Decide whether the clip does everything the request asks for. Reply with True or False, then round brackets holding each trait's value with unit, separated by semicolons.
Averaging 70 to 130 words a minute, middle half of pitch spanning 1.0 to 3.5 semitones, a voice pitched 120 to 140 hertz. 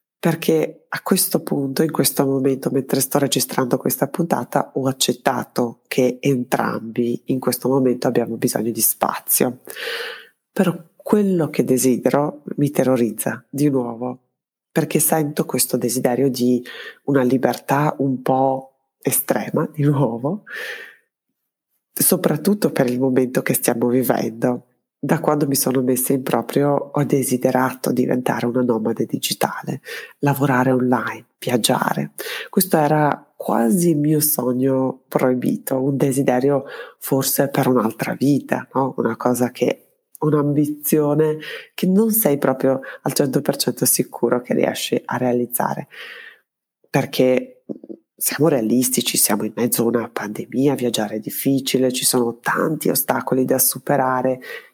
True (125 wpm; 2.5 semitones; 135 Hz)